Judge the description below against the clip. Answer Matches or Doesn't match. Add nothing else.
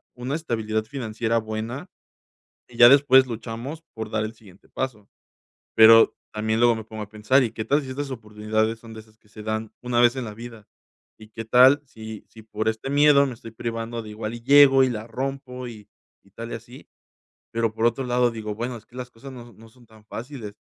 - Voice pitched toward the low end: Matches